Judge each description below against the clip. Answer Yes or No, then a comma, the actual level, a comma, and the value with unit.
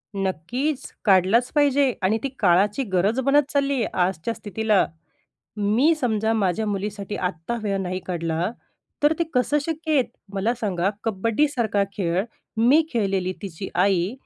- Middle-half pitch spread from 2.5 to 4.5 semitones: No, average, 5.0 semitones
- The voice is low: No, high, 210 Hz